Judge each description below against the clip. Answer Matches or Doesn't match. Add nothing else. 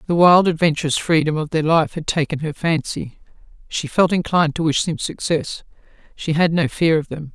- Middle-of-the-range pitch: Matches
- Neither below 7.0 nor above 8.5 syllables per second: Doesn't match